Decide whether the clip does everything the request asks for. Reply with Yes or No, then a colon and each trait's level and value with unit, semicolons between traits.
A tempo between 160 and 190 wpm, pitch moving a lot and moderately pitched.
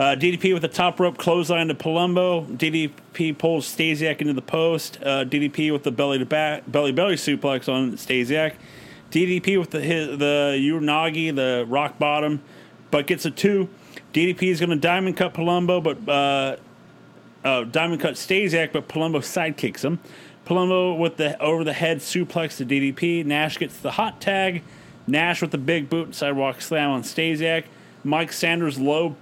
No: average, 170 wpm; average, 2.9 semitones; medium, 160 Hz